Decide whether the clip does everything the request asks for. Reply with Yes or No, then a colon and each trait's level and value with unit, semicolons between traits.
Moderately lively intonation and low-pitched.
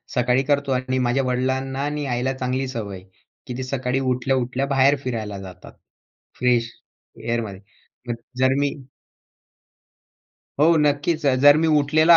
No: narrow, 1.9 semitones; low, 130 Hz